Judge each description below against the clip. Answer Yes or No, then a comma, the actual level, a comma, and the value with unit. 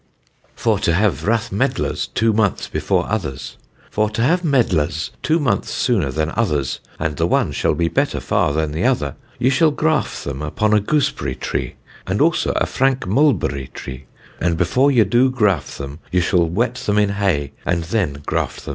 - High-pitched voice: No, low, 100 Hz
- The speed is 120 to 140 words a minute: No, average, 185 wpm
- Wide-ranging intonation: Yes, wide, 7.5 semitones